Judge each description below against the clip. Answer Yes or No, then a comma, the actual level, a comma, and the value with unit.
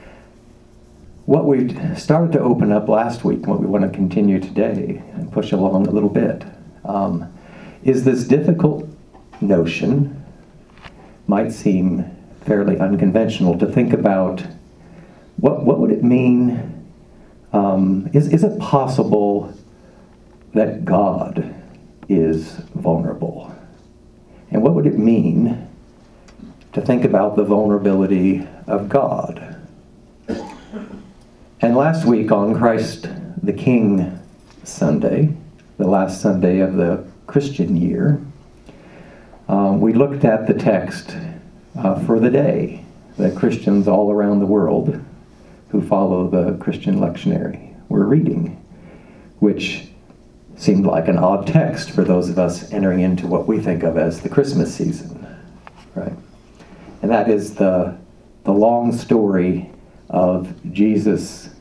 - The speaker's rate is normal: No, slow, 125 wpm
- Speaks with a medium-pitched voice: No, low, 105 Hz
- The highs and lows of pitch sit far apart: Yes, wide, 6.1 semitones